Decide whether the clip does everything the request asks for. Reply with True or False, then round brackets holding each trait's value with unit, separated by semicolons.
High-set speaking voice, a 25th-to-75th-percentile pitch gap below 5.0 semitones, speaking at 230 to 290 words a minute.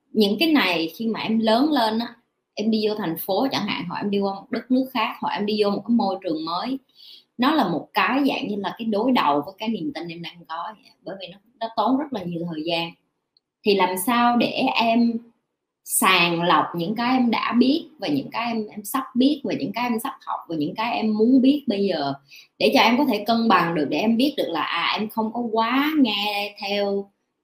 True (220 Hz; 4.1 semitones; 250 wpm)